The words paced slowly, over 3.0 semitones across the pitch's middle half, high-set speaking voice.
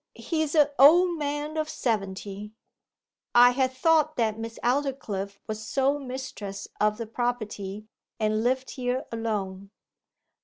Yes: slow, 125 wpm; average, 4.9 semitones; high, 245 Hz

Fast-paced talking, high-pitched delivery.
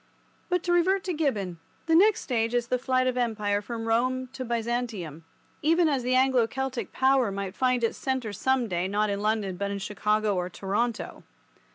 No: average, 190 wpm; high, 240 Hz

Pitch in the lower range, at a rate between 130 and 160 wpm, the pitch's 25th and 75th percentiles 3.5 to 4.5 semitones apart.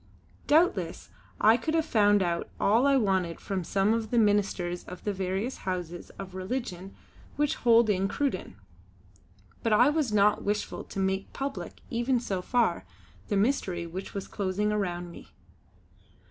No: high, 205 Hz; average, 155 wpm; average, 4.0 semitones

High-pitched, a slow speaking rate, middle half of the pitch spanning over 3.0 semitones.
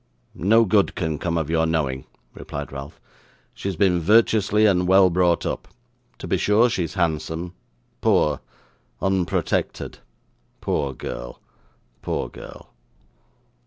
No: very low, 85 Hz; slow, 125 wpm; average, 3.7 semitones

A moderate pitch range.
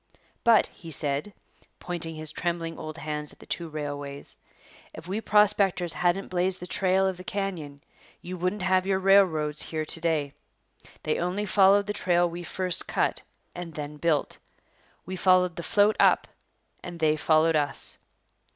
Yes: average, 3.3 semitones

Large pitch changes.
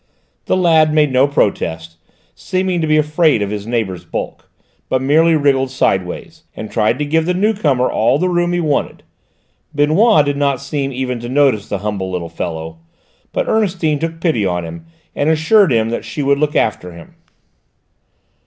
Yes: wide, 7.0 semitones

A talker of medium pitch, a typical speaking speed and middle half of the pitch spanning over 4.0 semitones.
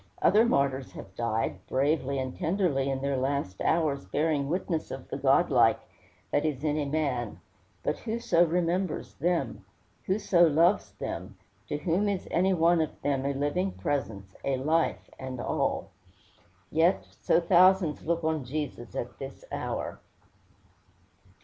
Yes: medium, 150 Hz; average, 145 wpm; average, 4.4 semitones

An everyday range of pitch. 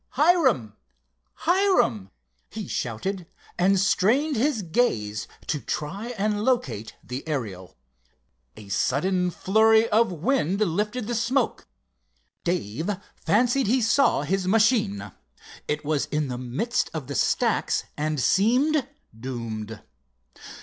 No: wide, 8.8 semitones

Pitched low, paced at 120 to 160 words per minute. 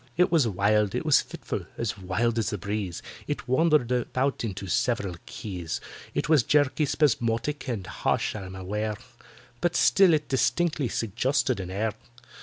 Yes: low, 115 Hz; average, 145 wpm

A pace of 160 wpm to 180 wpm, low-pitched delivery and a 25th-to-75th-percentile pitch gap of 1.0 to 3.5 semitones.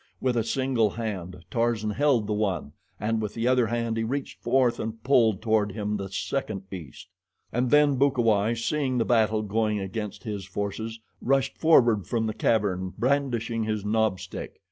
Yes: average, 170 wpm; low, 110 Hz; average, 2.8 semitones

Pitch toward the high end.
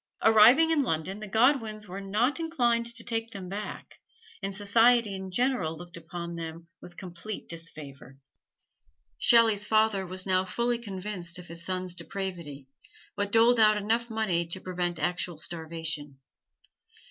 Yes: high, 195 Hz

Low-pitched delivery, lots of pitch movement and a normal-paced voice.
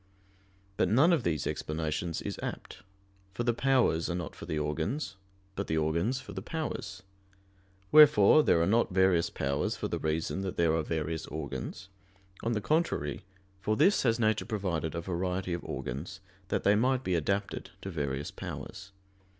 Yes: very low, 95 Hz; wide, 5.9 semitones; average, 170 wpm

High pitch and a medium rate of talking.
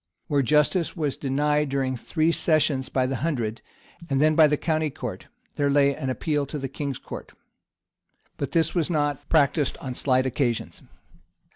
No: medium, 145 Hz; average, 170 wpm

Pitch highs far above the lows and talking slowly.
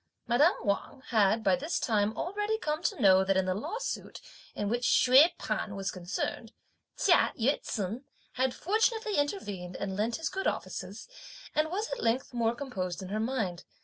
No: wide, 7.5 semitones; average, 175 wpm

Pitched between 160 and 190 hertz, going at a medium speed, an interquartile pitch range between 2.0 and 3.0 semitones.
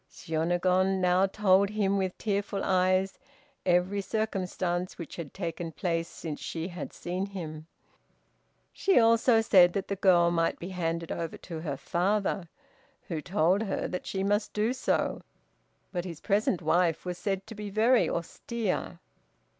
Yes: medium, 185 Hz; average, 150 wpm; average, 2.7 semitones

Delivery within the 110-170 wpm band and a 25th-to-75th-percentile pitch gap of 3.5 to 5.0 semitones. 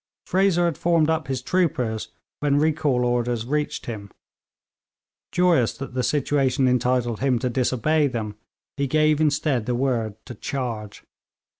Yes: average, 140 wpm; average, 3.9 semitones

